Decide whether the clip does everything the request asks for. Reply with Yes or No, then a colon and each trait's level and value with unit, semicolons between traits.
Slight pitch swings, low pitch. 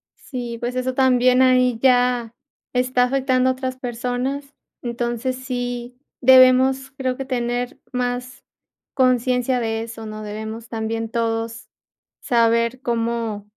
No: narrow, 1.7 semitones; high, 245 Hz